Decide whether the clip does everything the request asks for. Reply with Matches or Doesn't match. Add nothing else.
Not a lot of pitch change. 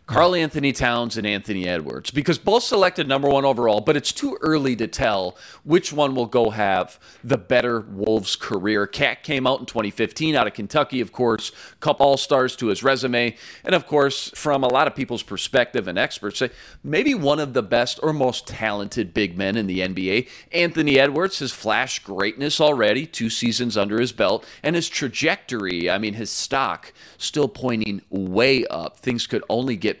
Doesn't match